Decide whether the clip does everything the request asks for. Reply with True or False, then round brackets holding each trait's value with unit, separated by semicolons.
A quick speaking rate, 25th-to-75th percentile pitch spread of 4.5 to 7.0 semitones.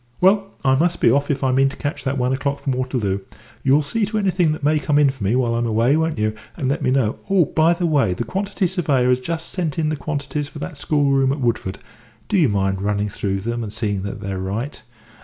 True (245 wpm; 5.0 semitones)